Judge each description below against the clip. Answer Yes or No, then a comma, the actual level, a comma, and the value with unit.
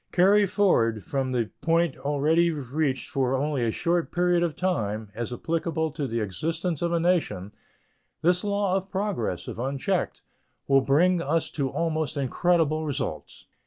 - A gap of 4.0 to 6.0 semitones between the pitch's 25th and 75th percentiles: Yes, average, 4.7 semitones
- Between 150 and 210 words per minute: Yes, average, 155 wpm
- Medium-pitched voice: Yes, medium, 155 Hz